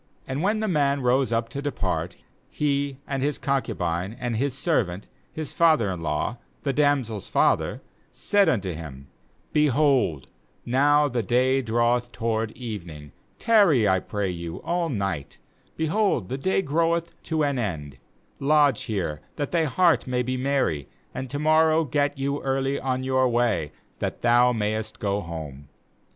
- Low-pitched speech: Yes, low, 130 Hz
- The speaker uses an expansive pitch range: Yes, wide, 5.9 semitones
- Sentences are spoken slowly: No, average, 155 wpm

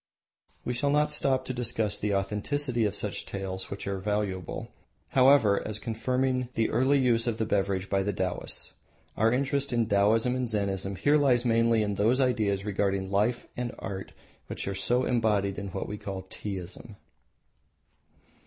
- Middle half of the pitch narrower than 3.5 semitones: No, average, 4.1 semitones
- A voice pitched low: Yes, low, 110 Hz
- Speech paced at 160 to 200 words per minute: Yes, average, 165 wpm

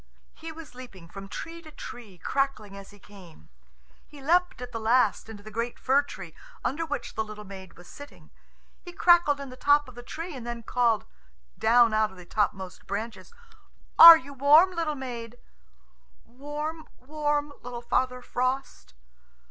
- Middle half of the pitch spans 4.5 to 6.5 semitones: Yes, wide, 5.4 semitones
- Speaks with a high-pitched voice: Yes, very high, 250 Hz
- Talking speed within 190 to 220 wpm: No, average, 165 wpm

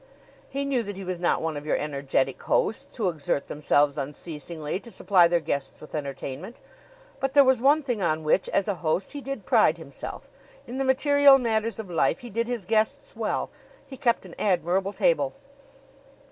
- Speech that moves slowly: No, average, 190 wpm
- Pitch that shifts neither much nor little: No, wide, 8.4 semitones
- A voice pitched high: Yes, high, 195 Hz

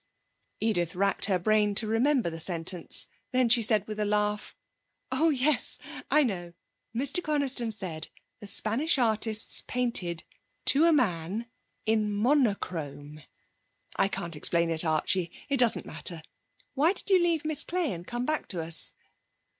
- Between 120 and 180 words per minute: Yes, average, 150 wpm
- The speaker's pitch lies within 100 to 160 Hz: No, high, 215 Hz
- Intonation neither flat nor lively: No, wide, 7.0 semitones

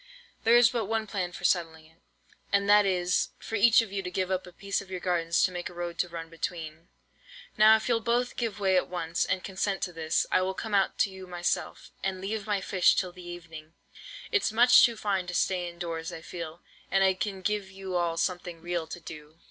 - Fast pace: Yes, fast, 235 wpm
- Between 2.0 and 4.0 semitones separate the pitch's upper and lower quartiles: Yes, average, 2.7 semitones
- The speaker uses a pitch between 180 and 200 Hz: Yes, medium, 185 Hz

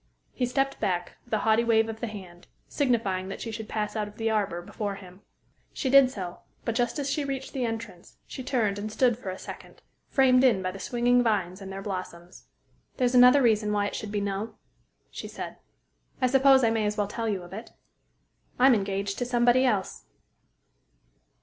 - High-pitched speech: Yes, high, 220 Hz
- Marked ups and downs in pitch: No, average, 3.8 semitones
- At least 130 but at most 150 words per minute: No, average, 200 wpm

